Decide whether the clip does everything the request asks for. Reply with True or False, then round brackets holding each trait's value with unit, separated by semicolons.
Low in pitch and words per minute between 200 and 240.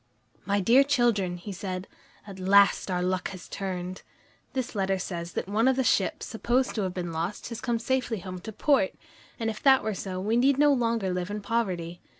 False (200 Hz; 205 wpm)